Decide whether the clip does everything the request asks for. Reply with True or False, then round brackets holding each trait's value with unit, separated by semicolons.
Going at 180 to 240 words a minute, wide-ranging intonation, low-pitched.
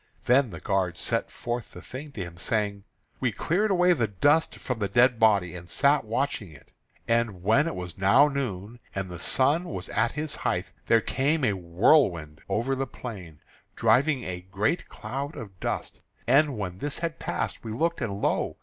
True (185 wpm; 6.6 semitones; 115 Hz)